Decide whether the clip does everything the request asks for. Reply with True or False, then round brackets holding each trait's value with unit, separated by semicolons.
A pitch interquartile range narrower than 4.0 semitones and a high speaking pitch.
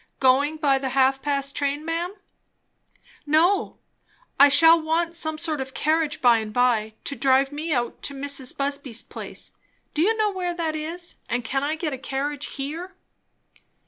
True (3.3 semitones; 290 Hz)